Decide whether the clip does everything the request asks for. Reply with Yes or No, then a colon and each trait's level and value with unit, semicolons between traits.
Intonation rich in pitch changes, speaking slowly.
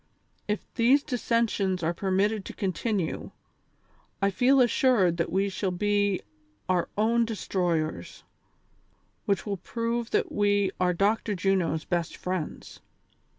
No: average, 3.6 semitones; slow, 120 wpm